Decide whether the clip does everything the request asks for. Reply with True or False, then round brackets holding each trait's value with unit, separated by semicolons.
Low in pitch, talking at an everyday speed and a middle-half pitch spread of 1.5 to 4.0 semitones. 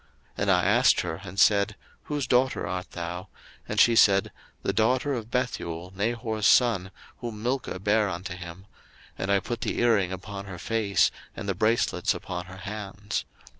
True (100 Hz; 170 wpm; 3.7 semitones)